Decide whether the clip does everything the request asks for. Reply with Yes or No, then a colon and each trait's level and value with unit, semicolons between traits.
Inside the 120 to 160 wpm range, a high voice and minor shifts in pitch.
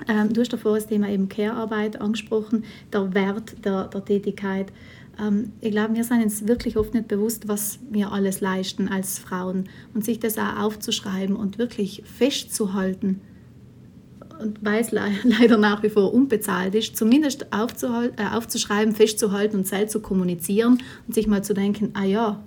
Yes: average, 155 wpm; high, 210 Hz; narrow, 1.9 semitones